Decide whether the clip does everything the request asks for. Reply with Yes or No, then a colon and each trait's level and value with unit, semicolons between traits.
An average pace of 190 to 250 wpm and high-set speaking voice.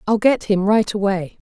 Yes: fast, 205 wpm; high, 205 Hz